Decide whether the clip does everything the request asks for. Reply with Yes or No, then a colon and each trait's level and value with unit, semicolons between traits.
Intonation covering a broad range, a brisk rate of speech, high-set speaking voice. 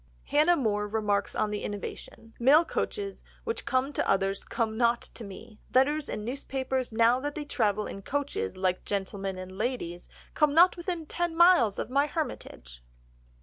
No: wide, 6.2 semitones; average, 165 wpm; high, 240 Hz